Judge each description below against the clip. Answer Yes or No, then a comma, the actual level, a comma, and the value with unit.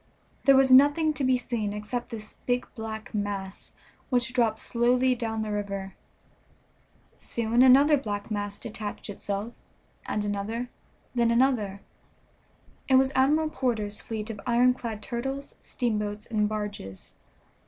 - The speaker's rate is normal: No, slow, 130 wpm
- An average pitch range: Yes, average, 3.4 semitones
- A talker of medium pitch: No, high, 230 Hz